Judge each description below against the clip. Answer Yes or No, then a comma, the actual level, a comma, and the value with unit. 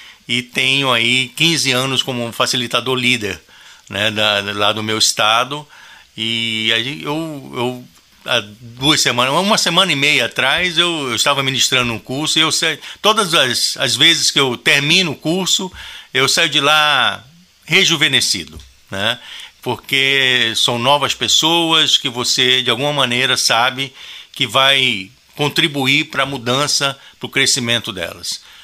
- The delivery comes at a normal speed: Yes, average, 140 wpm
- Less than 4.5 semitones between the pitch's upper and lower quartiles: Yes, average, 4.0 semitones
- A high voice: No, low, 135 Hz